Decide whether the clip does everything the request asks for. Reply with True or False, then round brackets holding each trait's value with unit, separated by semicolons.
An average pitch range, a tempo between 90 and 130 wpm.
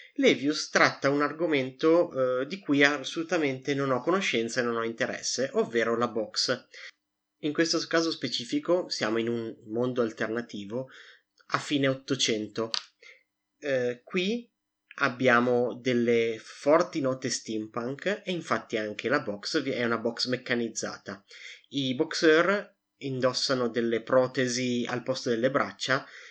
True (4.0 semitones; 125 wpm)